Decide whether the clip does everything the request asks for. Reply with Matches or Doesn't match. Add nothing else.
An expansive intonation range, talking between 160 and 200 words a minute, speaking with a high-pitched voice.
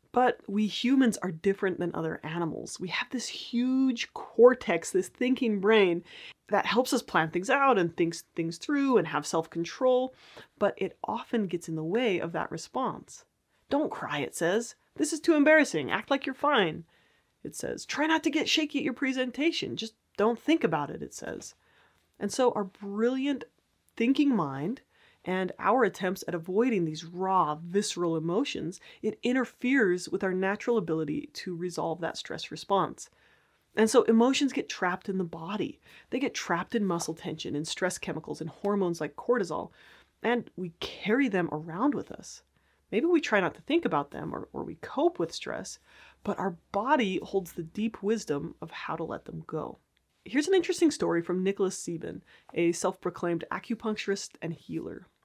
Matches